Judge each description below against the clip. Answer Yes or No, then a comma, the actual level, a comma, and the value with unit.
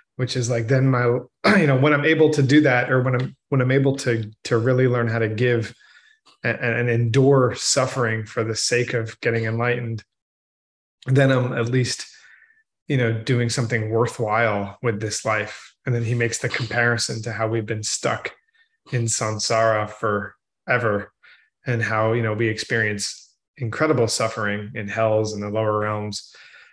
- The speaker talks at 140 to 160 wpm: No, average, 170 wpm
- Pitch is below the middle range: Yes, low, 120 Hz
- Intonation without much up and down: Yes, narrow, 2.3 semitones